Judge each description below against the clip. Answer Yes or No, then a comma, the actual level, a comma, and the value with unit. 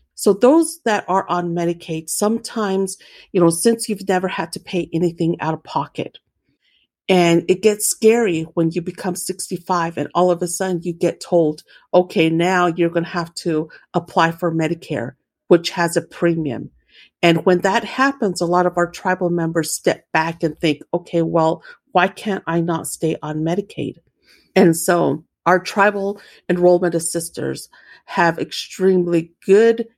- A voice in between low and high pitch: Yes, medium, 175 Hz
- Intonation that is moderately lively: No, narrow, 2.3 semitones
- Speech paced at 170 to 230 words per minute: No, average, 160 wpm